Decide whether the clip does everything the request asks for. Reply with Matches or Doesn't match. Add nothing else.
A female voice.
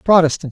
Doesn't match